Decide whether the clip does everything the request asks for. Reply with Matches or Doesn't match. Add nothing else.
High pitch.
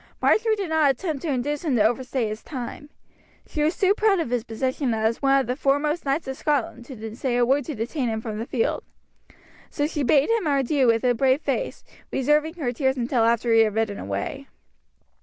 Matches